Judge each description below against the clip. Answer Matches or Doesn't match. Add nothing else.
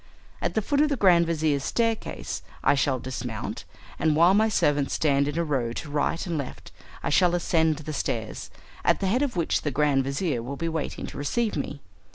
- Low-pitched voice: Doesn't match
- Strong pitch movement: Doesn't match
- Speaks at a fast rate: Matches